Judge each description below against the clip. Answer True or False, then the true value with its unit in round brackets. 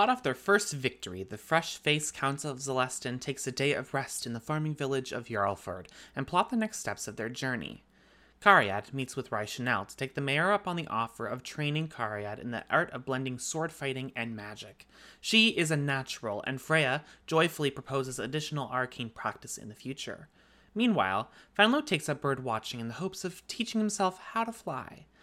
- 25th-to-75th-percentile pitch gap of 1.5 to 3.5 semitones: False (4.7 semitones)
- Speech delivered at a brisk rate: False (195 wpm)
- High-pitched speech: False (135 Hz)